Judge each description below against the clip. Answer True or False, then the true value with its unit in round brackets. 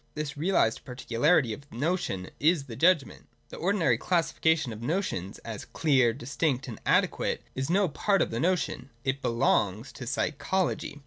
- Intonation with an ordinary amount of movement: False (5.8 semitones)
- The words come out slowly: False (155 wpm)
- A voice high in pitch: False (140 Hz)